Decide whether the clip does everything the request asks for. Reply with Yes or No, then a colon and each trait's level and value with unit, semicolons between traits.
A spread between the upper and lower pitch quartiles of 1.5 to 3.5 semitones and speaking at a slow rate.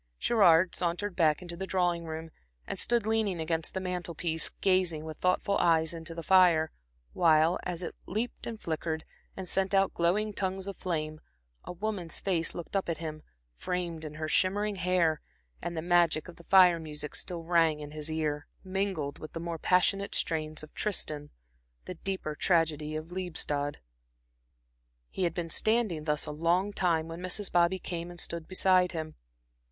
No: average, 2.7 semitones; average, 175 wpm